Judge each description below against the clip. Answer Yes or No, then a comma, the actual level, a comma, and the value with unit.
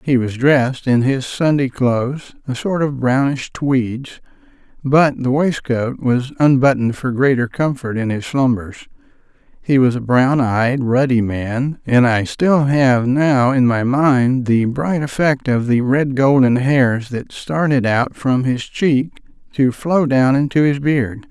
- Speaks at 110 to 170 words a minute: Yes, average, 165 wpm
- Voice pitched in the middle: No, low, 130 Hz